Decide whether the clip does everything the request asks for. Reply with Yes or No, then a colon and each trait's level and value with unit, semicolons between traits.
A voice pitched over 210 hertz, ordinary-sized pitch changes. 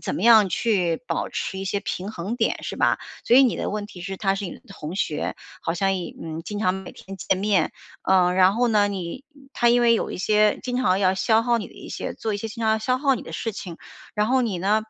No: high, 205 Hz; average, 3.3 semitones